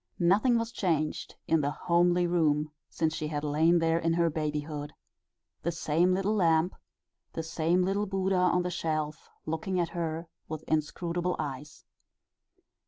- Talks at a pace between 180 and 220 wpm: No, average, 150 wpm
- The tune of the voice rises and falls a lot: No, narrow, 2.5 semitones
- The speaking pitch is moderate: Yes, medium, 165 Hz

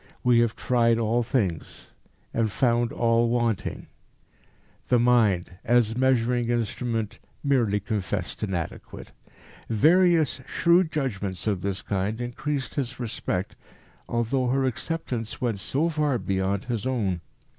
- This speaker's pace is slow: Yes, slow, 120 wpm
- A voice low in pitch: Yes, low, 115 Hz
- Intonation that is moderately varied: Yes, average, 3.6 semitones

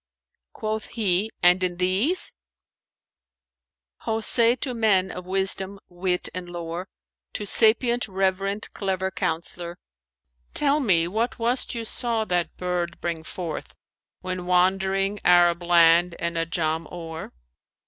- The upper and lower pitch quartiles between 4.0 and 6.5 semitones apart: No, average, 3.6 semitones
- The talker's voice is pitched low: No, medium, 185 Hz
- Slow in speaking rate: Yes, slow, 130 wpm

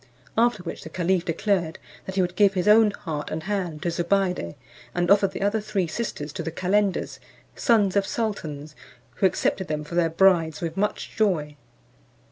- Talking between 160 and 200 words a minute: Yes, average, 180 wpm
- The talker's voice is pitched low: No, medium, 185 Hz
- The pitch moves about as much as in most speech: Yes, average, 3.7 semitones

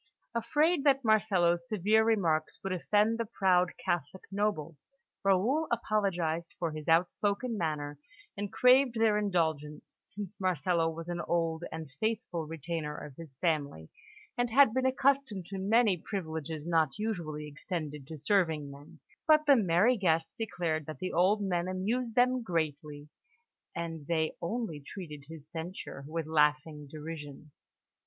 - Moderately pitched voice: Yes, medium, 175 Hz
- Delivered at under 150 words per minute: Yes, average, 140 wpm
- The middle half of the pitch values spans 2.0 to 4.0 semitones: No, average, 5.3 semitones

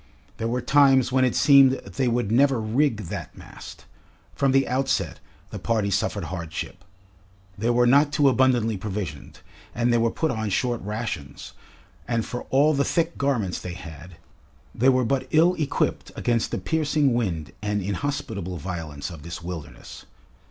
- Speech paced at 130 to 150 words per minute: No, average, 160 wpm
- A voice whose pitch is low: Yes, low, 115 Hz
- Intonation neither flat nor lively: No, wide, 6.3 semitones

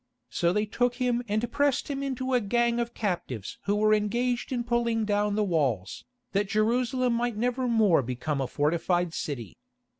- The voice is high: Yes, high, 215 Hz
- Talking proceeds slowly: No, average, 170 wpm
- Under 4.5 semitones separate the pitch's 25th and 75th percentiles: No, wide, 5.4 semitones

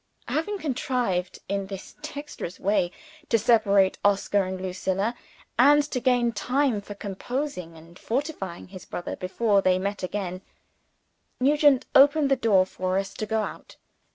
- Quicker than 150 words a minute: No, average, 145 wpm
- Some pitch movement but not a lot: No, wide, 5.8 semitones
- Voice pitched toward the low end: No, high, 205 Hz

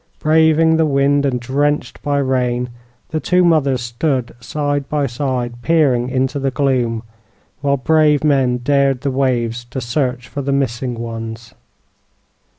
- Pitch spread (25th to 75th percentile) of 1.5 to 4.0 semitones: Yes, average, 2.8 semitones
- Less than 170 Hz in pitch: Yes, low, 135 Hz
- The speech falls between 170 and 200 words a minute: No, average, 145 wpm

